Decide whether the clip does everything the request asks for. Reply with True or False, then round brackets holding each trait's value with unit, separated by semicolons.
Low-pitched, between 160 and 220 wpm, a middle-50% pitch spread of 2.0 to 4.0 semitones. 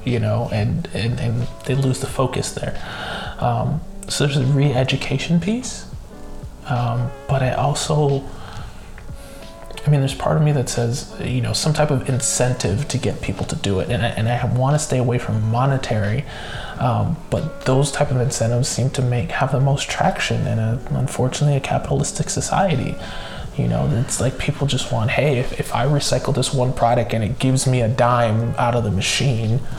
True (125 Hz; 190 wpm; 2.9 semitones)